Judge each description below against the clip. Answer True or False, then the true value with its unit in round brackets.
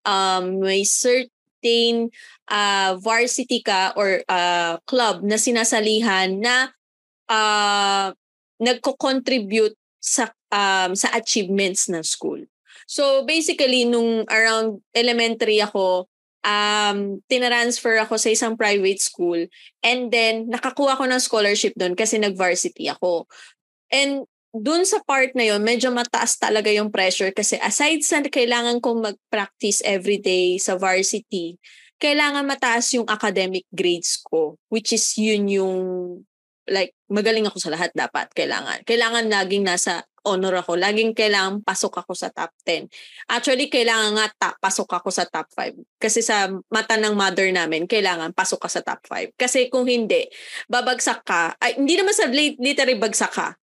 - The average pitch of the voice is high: True (220 Hz)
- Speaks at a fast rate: False (140 wpm)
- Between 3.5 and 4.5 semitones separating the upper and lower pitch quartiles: True (4.2 semitones)